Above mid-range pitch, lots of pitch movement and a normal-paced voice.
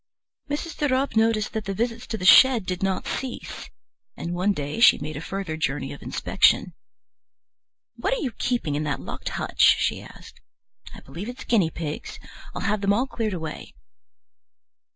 Yes: high, 200 Hz; wide, 6.4 semitones; average, 175 wpm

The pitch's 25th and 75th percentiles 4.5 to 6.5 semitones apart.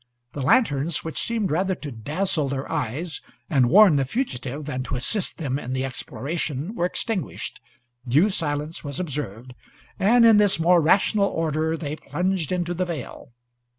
Yes: average, 5.2 semitones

